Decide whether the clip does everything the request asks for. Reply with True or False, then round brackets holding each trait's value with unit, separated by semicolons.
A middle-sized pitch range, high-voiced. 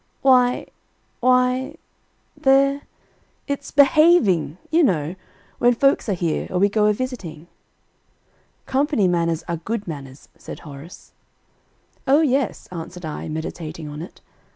False (8.5 semitones; 205 Hz)